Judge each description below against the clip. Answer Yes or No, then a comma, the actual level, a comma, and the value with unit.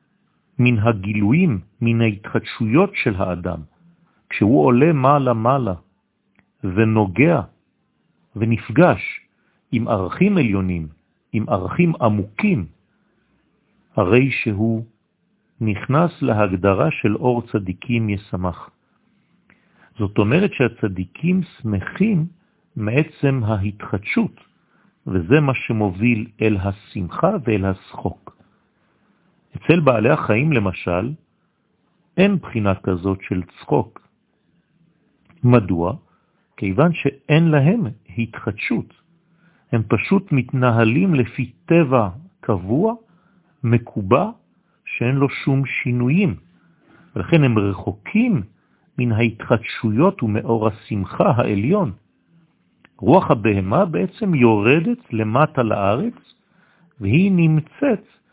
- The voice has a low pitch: Yes, low, 120 Hz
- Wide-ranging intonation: Yes, wide, 7.9 semitones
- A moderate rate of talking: No, slow, 80 wpm